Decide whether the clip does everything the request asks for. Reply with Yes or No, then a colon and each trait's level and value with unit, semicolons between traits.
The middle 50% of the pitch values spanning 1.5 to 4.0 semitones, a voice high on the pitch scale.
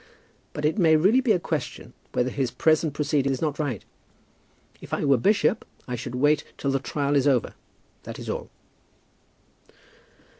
No: average, 2.8 semitones; medium, 145 Hz